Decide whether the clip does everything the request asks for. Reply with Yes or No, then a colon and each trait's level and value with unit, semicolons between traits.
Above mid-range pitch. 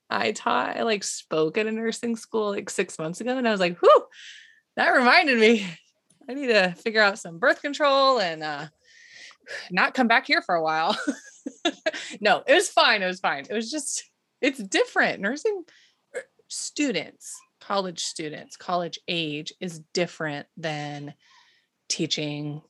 Yes: high, 225 Hz